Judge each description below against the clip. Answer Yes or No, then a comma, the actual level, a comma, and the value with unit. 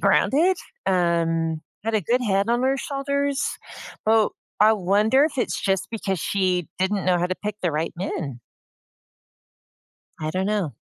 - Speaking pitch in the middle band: No, high, 195 Hz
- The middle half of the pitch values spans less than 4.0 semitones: No, average, 5.2 semitones